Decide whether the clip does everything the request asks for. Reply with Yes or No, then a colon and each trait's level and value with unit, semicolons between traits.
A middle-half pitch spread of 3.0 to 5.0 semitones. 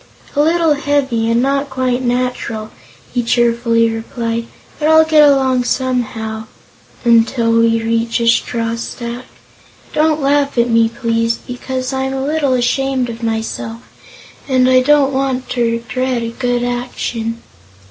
No: narrow, 2.5 semitones